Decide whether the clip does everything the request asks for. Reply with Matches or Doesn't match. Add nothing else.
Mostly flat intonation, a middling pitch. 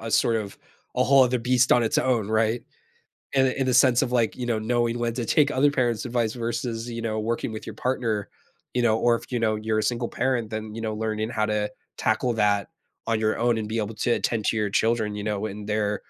Doesn't match